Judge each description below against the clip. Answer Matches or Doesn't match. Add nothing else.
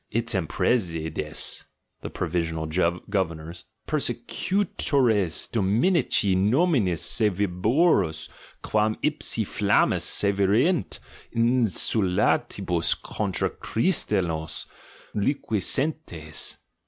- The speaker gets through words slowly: Matches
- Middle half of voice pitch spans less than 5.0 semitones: Doesn't match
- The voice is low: Matches